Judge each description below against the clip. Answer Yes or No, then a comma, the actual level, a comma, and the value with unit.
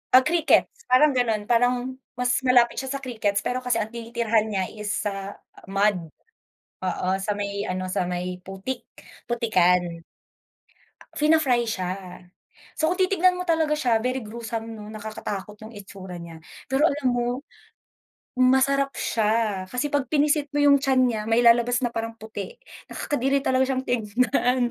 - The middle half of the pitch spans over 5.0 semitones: No, average, 4.0 semitones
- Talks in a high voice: Yes, high, 235 Hz